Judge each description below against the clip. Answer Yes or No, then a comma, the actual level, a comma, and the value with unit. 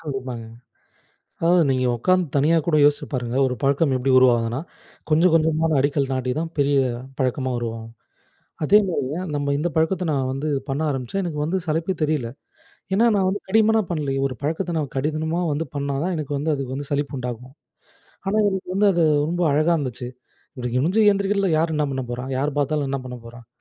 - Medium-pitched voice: Yes, medium, 145 Hz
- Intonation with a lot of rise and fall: No, average, 4.2 semitones